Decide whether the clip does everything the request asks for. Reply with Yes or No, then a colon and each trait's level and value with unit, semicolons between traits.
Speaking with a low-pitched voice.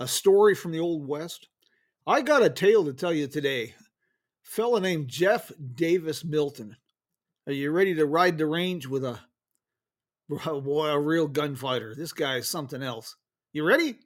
No: medium, 160 Hz